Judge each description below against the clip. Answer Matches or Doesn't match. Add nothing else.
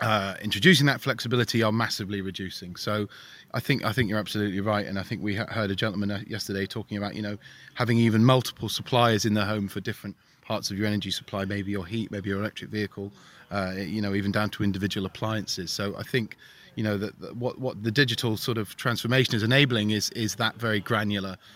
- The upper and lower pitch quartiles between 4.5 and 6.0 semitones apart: Doesn't match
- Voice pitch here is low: Matches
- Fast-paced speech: Matches